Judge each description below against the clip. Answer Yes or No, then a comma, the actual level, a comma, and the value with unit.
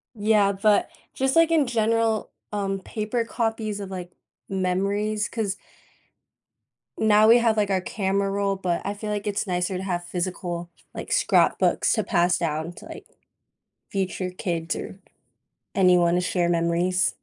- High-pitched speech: Yes, high, 195 Hz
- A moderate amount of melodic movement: Yes, average, 3.0 semitones